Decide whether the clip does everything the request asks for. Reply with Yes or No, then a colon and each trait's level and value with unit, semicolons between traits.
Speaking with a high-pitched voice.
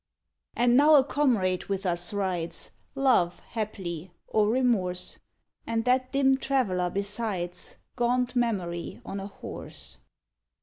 Yes: high, 210 Hz